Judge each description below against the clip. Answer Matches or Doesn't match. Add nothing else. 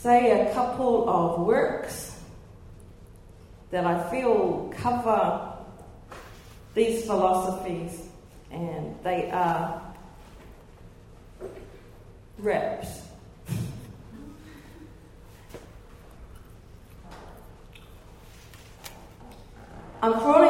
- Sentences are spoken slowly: Matches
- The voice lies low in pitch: Doesn't match